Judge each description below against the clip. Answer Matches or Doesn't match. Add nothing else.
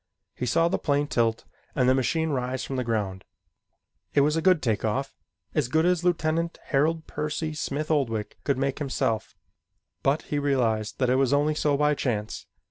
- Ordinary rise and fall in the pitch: Matches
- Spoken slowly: Doesn't match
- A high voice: Doesn't match